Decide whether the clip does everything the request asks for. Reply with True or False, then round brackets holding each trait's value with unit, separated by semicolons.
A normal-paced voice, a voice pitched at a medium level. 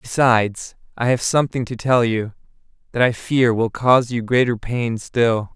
False (175 wpm; 120 Hz)